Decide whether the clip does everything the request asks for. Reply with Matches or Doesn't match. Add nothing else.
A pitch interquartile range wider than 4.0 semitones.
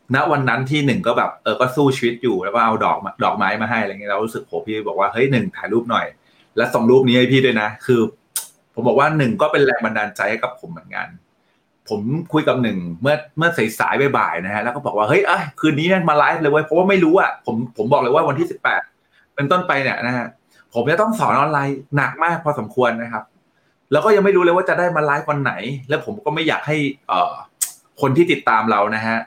Matches